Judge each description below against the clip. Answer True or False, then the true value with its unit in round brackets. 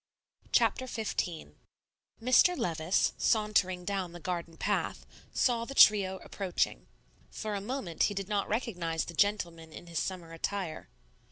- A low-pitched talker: False (190 Hz)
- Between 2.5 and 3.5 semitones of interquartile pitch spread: False (3.9 semitones)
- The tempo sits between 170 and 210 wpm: False (140 wpm)